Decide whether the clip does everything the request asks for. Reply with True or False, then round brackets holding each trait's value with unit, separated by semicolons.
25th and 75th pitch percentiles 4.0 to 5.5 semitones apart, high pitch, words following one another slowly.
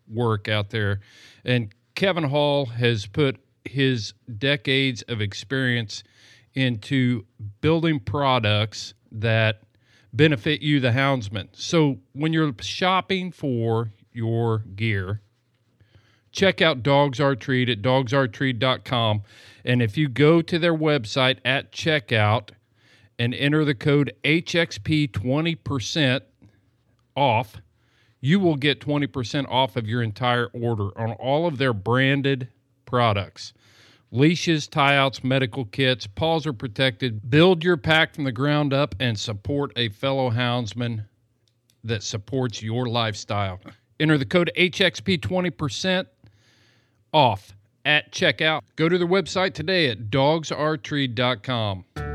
False (4.4 semitones; 125 Hz; 115 wpm)